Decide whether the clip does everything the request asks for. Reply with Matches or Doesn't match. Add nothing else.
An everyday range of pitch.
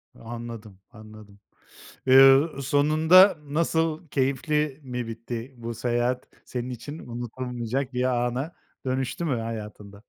Matches